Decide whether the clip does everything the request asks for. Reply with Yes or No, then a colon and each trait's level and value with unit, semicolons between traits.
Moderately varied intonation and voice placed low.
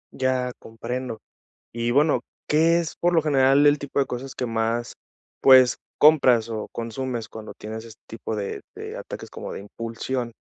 Yes: average, 3.1 semitones; low, 125 Hz